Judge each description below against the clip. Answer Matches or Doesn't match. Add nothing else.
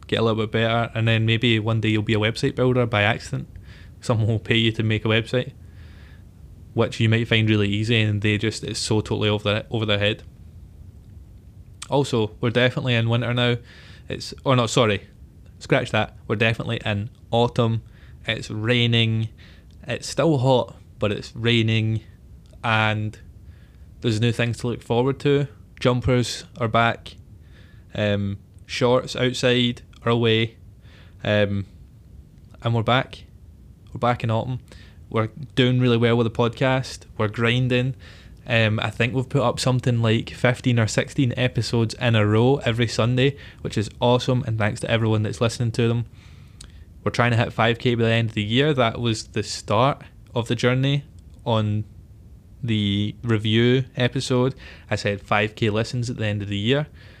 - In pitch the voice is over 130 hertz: Doesn't match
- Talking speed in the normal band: Matches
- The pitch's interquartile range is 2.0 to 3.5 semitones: Matches